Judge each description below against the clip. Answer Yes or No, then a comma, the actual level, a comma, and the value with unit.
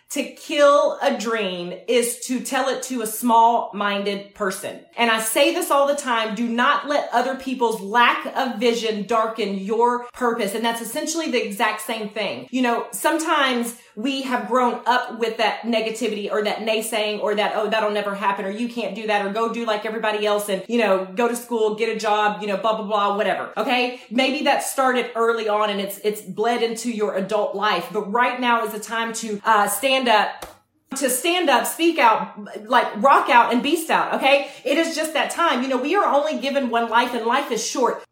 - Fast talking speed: Yes, fast, 215 wpm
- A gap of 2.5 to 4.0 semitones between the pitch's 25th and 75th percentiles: Yes, average, 3.2 semitones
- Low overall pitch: No, high, 230 Hz